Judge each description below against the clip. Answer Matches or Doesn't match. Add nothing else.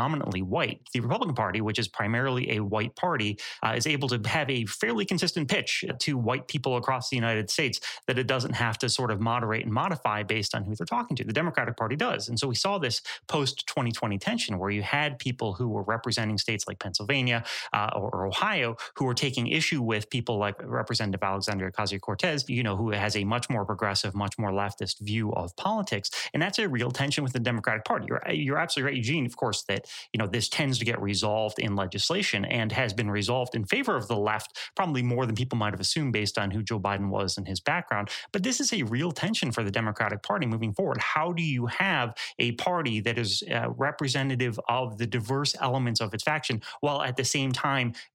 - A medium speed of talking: Doesn't match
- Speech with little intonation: Doesn't match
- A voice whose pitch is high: Doesn't match